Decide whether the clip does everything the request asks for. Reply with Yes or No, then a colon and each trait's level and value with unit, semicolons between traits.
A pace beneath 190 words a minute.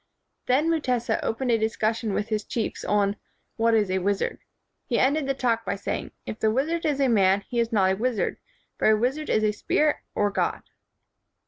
No: average, 200 wpm